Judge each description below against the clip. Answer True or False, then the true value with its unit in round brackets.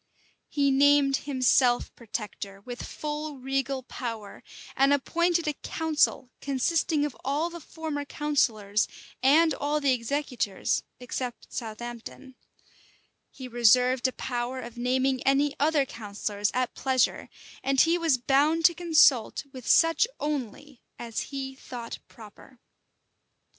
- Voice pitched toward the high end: True (270 Hz)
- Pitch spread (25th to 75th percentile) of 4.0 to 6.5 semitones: False (3.4 semitones)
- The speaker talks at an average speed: False (120 wpm)